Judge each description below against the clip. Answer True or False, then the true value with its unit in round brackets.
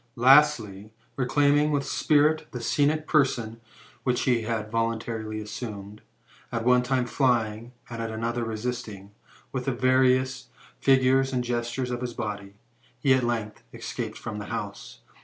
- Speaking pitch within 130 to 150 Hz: False (120 Hz)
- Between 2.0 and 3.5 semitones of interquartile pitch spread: True (2.9 semitones)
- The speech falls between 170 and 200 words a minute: False (140 wpm)